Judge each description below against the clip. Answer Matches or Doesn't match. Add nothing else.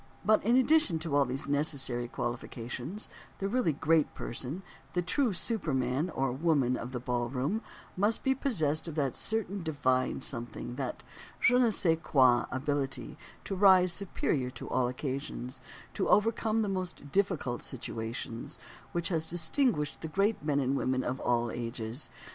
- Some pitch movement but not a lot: Doesn't match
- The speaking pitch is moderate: Matches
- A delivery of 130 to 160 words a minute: Matches